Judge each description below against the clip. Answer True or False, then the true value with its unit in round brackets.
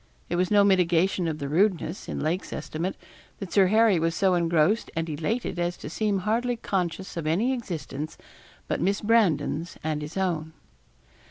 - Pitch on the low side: False (180 Hz)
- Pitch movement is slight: False (3.7 semitones)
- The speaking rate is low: False (170 wpm)